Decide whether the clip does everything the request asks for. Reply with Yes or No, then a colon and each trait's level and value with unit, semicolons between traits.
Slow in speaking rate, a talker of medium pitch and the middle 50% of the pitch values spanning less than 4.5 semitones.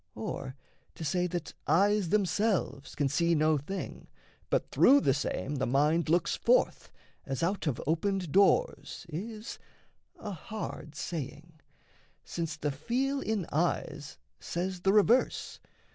No: slow, 130 wpm; medium, 170 Hz; average, 5.2 semitones